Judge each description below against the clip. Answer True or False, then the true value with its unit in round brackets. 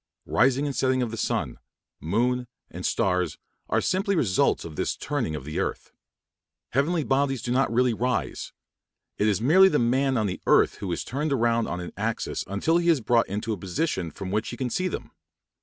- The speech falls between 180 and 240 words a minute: True (195 wpm)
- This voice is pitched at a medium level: False (120 Hz)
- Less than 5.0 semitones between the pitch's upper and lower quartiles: False (5.5 semitones)